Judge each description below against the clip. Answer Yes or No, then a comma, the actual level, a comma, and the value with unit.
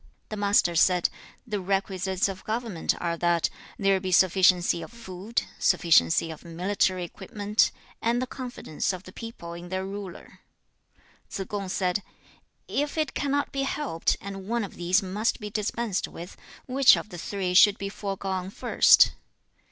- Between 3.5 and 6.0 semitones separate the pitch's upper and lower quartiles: No, average, 3.0 semitones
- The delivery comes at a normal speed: Yes, average, 160 wpm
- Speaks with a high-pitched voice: Yes, high, 195 Hz